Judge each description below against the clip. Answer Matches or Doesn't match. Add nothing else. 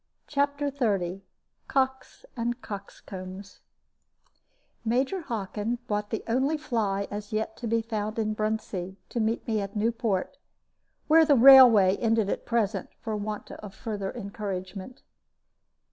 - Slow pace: Matches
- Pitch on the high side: Matches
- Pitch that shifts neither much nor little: Matches